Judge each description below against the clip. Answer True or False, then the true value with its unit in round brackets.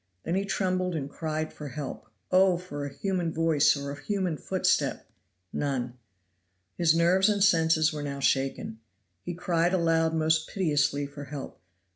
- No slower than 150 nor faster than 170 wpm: True (160 wpm)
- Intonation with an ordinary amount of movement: True (3.8 semitones)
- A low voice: False (160 Hz)